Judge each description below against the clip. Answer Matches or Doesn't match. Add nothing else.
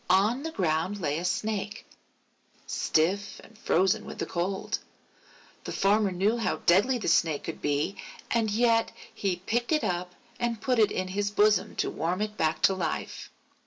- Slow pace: Doesn't match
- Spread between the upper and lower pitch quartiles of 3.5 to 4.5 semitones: Matches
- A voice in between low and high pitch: Doesn't match